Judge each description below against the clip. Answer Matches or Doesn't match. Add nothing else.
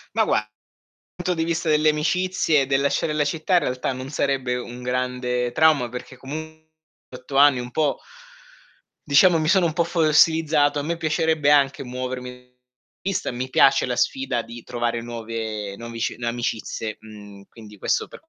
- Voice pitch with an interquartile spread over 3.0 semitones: Matches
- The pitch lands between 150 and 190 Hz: Doesn't match